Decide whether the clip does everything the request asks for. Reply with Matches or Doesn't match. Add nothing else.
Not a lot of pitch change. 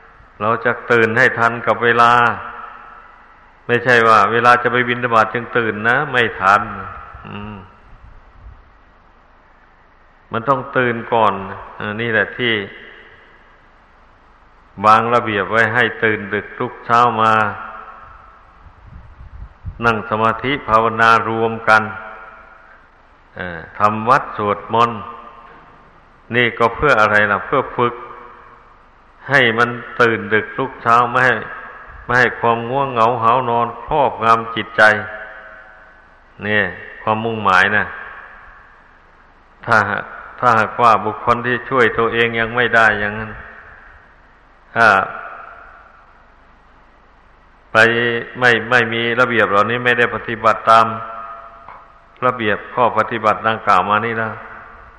Matches